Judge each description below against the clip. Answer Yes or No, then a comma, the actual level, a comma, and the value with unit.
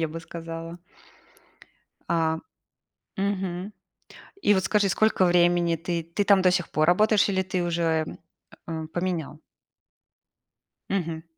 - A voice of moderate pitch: Yes, medium, 175 Hz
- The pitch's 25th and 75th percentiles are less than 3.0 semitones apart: Yes, narrow, 2.4 semitones